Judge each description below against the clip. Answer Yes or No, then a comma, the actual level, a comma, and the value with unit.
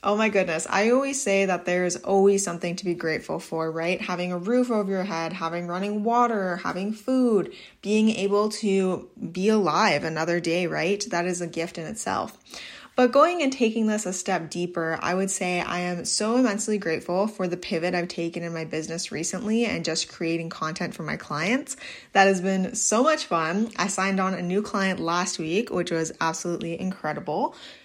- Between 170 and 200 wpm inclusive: Yes, average, 195 wpm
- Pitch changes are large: No, average, 3.8 semitones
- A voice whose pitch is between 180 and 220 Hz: Yes, medium, 185 Hz